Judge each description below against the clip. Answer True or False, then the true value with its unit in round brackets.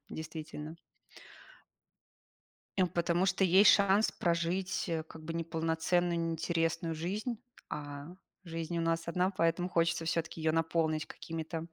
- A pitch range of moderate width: False (1.4 semitones)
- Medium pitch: True (165 Hz)